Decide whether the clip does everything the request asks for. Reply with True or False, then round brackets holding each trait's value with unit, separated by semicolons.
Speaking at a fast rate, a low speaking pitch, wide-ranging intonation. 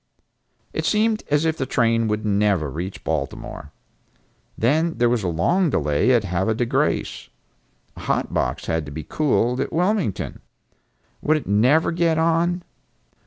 False (155 wpm; 120 Hz; 9.0 semitones)